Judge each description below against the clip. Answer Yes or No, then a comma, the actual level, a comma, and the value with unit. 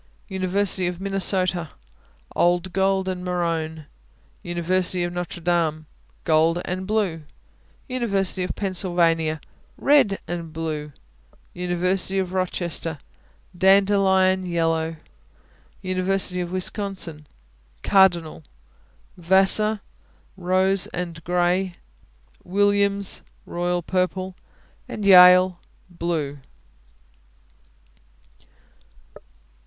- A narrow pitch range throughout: Yes, narrow, 1.9 semitones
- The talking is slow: Yes, slow, 75 wpm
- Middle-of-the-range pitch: Yes, medium, 180 Hz